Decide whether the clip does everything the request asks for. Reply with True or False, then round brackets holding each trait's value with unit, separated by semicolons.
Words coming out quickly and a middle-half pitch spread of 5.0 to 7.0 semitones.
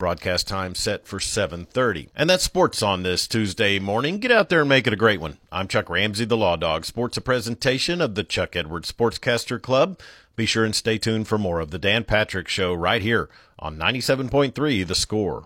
True (225 wpm; 5.3 semitones)